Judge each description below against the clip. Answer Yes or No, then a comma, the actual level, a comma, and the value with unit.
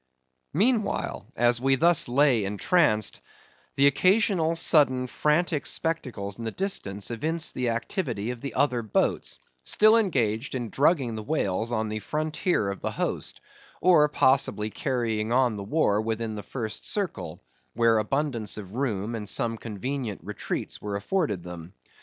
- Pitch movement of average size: No, wide, 5.9 semitones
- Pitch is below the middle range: Yes, low, 120 Hz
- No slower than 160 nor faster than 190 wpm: No, average, 145 wpm